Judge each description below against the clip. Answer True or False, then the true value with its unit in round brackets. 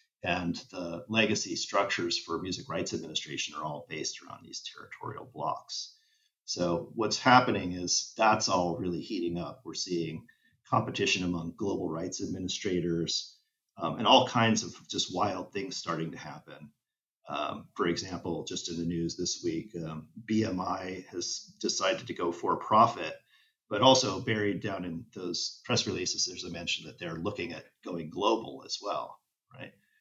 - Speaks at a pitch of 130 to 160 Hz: False (95 Hz)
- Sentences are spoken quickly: False (160 wpm)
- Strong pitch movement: True (7.4 semitones)